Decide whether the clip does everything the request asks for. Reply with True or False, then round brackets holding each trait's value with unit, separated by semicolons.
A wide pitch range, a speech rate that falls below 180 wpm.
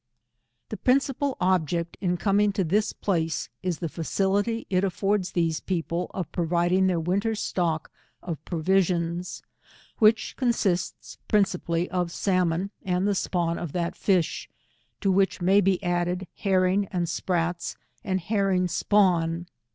False (2.4 semitones; 135 wpm)